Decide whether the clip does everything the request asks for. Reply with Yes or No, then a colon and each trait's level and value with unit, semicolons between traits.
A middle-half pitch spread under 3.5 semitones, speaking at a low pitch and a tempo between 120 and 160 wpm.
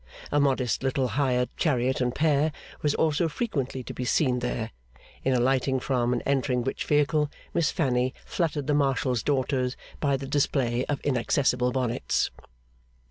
Yes: narrow, 2.6 semitones; low, 130 Hz; average, 150 wpm